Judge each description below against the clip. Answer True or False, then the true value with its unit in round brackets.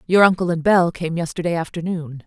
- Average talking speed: True (185 wpm)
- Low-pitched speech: False (170 Hz)